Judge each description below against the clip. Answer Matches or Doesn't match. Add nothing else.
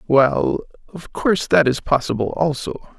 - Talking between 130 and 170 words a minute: Matches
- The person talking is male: Matches